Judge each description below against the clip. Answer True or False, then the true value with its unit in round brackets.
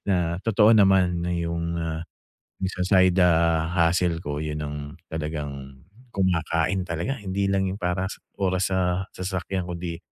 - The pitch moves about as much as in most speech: False (2.3 semitones)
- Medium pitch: False (90 Hz)